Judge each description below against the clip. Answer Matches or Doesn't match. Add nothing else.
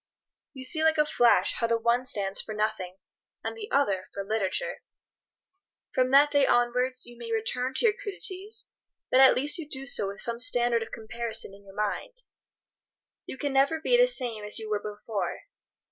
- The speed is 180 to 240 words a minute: Matches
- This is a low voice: Doesn't match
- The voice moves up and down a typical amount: Matches